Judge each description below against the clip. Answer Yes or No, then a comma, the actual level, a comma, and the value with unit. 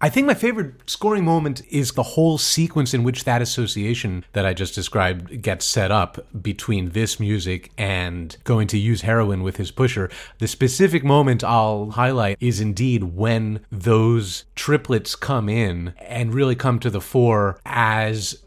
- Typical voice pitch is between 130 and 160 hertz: No, low, 115 Hz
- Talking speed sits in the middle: Yes, average, 165 wpm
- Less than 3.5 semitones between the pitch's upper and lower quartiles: No, average, 3.9 semitones